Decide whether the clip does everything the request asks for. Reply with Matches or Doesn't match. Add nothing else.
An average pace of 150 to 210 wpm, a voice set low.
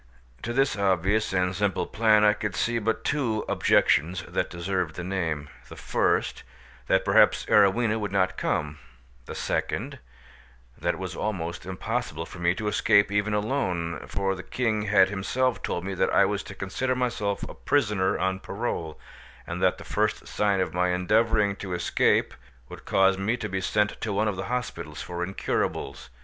Matches